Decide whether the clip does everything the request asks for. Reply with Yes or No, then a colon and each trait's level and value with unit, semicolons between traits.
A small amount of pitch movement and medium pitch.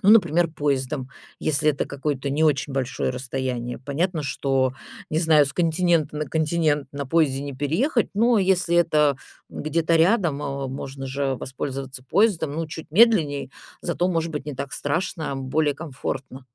No: average, 3.5 semitones; medium, 150 Hz